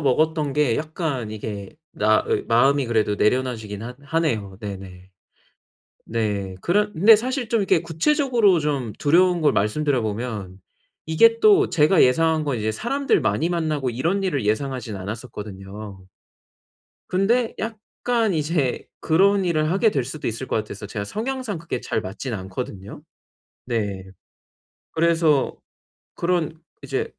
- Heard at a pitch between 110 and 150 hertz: Yes, medium, 140 Hz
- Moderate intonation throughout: No, wide, 8.2 semitones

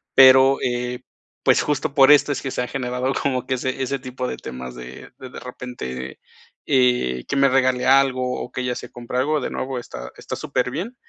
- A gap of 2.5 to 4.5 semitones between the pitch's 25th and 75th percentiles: No, narrow, 1.5 semitones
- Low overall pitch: Yes, low, 130 Hz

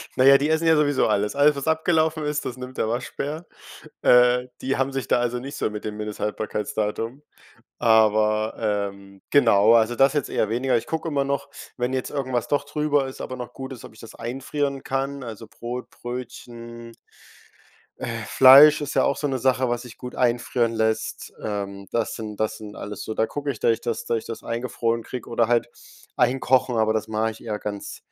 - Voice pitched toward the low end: Yes, low, 120 Hz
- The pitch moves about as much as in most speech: Yes, average, 3.6 semitones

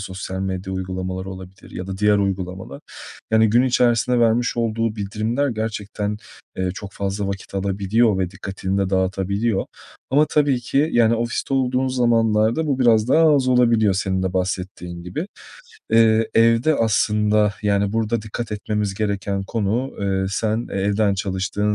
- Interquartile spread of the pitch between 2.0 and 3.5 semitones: Yes, average, 3.2 semitones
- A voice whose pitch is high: No, low, 105 Hz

